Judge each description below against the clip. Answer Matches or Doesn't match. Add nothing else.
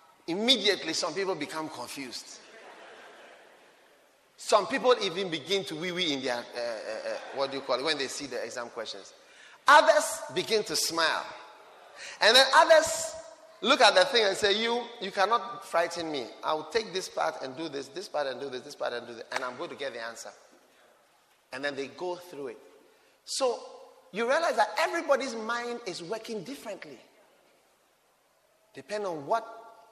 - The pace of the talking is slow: Doesn't match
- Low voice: Doesn't match